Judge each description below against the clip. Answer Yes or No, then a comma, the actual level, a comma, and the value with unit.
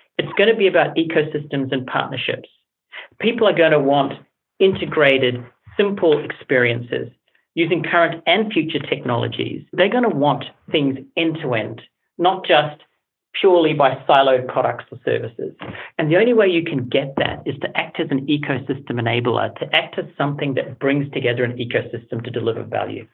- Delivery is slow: No, average, 165 wpm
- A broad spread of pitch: No, average, 4.7 semitones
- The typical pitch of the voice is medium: Yes, medium, 150 Hz